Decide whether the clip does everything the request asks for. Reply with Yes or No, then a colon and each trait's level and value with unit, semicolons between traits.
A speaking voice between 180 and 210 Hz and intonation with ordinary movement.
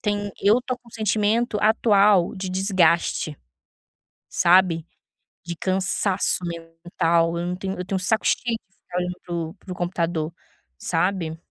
Yes: medium, 185 Hz; average, 3.2 semitones